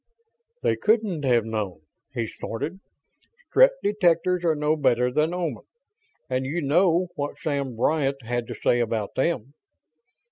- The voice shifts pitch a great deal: Yes, wide, 6.0 semitones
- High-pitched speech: No, medium, 145 Hz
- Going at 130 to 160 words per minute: Yes, average, 140 wpm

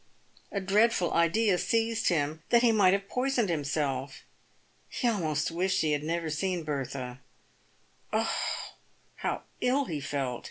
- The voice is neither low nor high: Yes, medium, 170 Hz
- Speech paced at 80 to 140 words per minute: Yes, slow, 135 wpm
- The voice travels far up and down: Yes, wide, 6.4 semitones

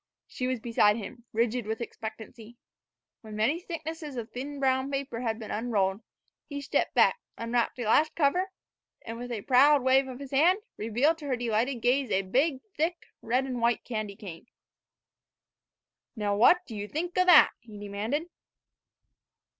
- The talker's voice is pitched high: Yes, high, 245 Hz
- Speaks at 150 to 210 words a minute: Yes, average, 165 wpm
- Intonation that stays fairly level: No, average, 4.3 semitones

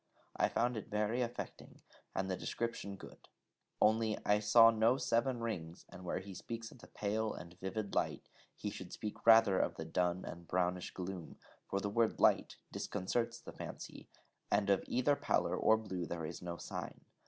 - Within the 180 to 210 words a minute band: Yes, average, 185 wpm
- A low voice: Yes, low, 105 Hz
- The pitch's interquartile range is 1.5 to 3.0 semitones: No, average, 3.8 semitones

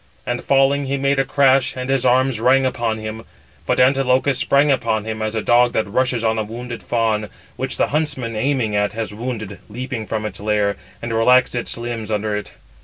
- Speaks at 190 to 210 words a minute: Yes, average, 200 wpm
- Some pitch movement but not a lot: Yes, average, 3.2 semitones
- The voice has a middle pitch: No, low, 120 Hz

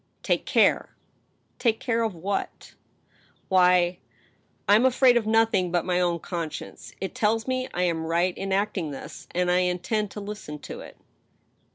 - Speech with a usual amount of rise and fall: Yes, average, 3.9 semitones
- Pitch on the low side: No, high, 190 Hz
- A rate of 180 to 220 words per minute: Yes, average, 185 wpm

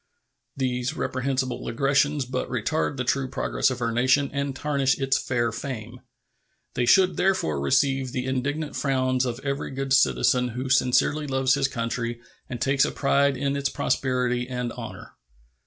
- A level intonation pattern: Yes, narrow, 1.9 semitones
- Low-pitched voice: Yes, low, 130 Hz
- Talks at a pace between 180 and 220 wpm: No, average, 155 wpm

